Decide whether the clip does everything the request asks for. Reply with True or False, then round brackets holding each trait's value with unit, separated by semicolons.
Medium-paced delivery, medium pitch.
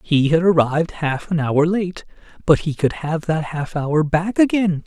True (195 wpm; 165 Hz)